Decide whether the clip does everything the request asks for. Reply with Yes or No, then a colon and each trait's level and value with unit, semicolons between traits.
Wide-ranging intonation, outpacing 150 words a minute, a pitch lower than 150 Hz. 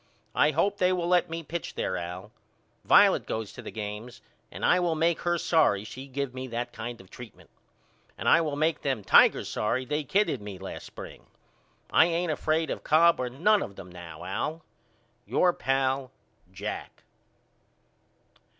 Yes: wide, 7.4 semitones; average, 170 wpm; low, 135 Hz